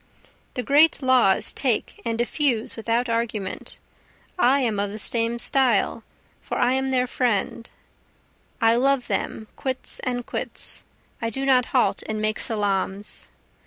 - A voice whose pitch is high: Yes, high, 235 Hz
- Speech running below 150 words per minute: Yes, average, 140 wpm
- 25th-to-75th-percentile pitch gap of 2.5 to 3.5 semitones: Yes, average, 3.0 semitones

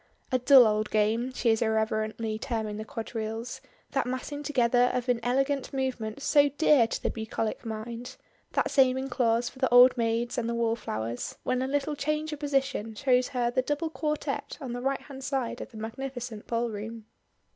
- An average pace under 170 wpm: No, average, 180 wpm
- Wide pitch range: No, average, 3.2 semitones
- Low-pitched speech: No, high, 245 Hz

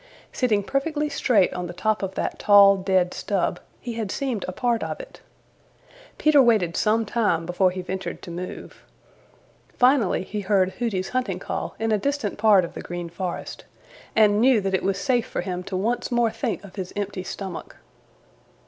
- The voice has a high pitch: Yes, high, 205 Hz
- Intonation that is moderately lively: Yes, average, 4.0 semitones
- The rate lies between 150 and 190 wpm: Yes, average, 185 wpm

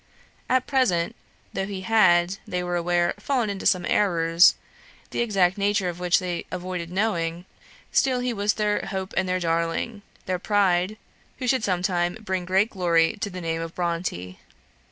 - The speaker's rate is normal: Yes, average, 170 wpm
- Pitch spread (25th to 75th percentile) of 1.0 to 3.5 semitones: Yes, average, 2.9 semitones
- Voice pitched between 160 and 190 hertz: Yes, medium, 185 Hz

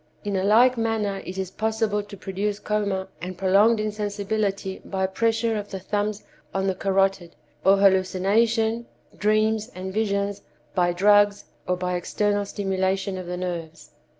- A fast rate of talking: No, average, 150 wpm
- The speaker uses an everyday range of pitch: No, narrow, 2.0 semitones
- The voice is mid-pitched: No, high, 200 Hz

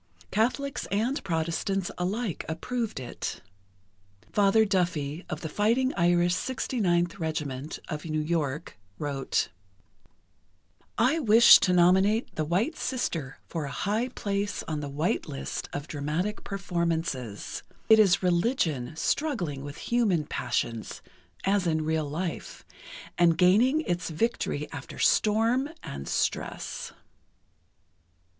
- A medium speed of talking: No, slow, 115 wpm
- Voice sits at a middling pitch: Yes, medium, 175 Hz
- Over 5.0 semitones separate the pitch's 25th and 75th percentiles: Yes, wide, 5.6 semitones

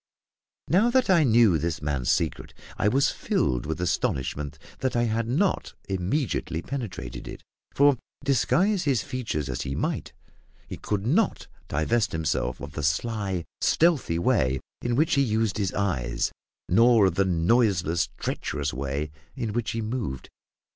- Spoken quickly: No, average, 150 wpm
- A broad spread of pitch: Yes, wide, 8.6 semitones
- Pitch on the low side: Yes, low, 105 Hz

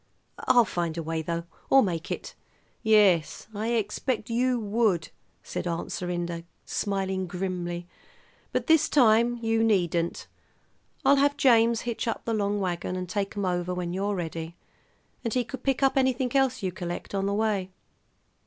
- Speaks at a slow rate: No, average, 160 wpm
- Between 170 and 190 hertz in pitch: No, high, 200 Hz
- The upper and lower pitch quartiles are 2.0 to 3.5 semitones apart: No, average, 4.8 semitones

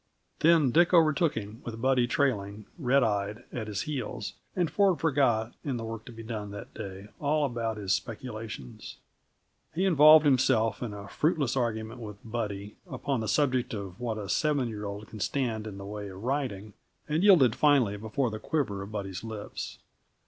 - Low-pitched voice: Yes, low, 115 Hz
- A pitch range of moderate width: Yes, average, 5.0 semitones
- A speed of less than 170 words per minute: No, average, 180 wpm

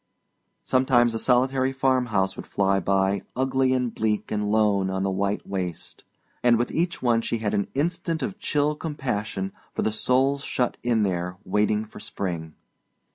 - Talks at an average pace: Yes, average, 165 wpm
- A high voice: No, low, 110 Hz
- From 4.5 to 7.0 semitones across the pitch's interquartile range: Yes, average, 4.9 semitones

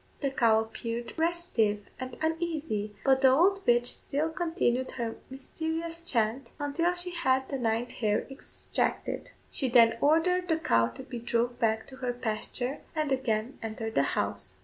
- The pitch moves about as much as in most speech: No, wide, 5.9 semitones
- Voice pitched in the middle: No, very high, 260 Hz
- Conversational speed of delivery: Yes, average, 160 wpm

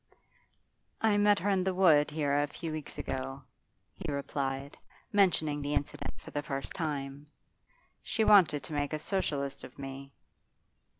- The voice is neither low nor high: Yes, medium, 145 Hz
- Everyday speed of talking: Yes, average, 155 wpm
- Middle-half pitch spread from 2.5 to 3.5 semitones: No, average, 4.4 semitones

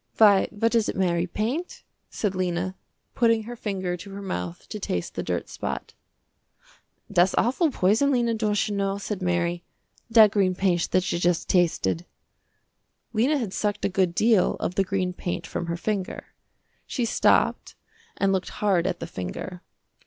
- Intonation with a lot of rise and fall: No, average, 3.4 semitones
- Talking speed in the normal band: Yes, average, 165 wpm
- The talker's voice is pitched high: Yes, high, 195 Hz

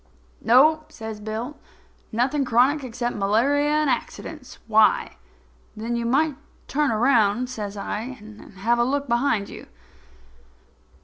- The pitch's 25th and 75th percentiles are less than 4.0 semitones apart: No, average, 4.3 semitones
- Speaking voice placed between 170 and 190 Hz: No, high, 240 Hz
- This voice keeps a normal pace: No, slow, 125 wpm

